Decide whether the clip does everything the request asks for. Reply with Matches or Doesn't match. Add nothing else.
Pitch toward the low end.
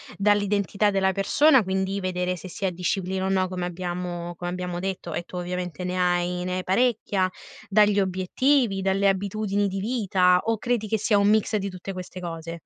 Doesn't match